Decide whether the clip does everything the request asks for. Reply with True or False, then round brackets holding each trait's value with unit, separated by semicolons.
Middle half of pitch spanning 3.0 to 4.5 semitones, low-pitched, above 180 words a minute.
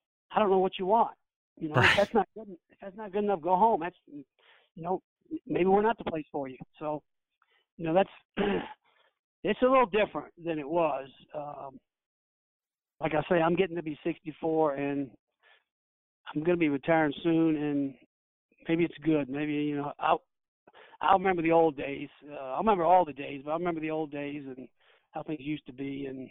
False (4.0 semitones; 155 Hz; 200 wpm)